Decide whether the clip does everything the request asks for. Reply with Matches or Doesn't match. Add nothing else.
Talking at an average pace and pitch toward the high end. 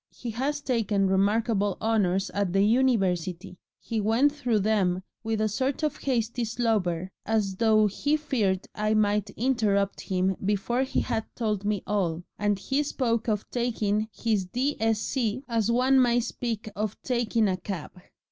Matches